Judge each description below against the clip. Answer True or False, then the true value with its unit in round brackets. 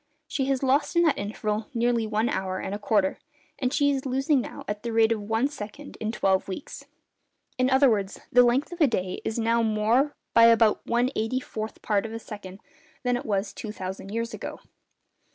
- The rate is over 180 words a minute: True (205 wpm)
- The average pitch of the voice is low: False (225 Hz)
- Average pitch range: True (3.6 semitones)